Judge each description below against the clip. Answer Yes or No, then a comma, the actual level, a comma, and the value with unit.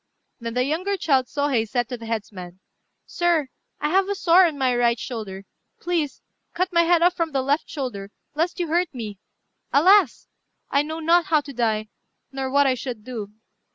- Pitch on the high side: Yes, very high, 280 Hz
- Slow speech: No, average, 190 wpm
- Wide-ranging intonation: Yes, wide, 6.1 semitones